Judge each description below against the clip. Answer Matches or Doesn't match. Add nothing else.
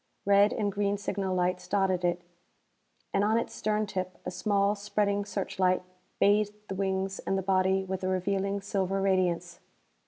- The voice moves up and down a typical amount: Doesn't match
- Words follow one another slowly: Doesn't match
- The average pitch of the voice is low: Doesn't match